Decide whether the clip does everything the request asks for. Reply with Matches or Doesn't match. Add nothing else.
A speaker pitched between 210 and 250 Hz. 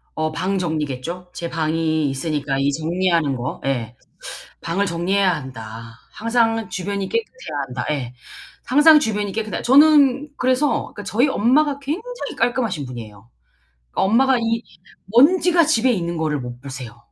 Doesn't match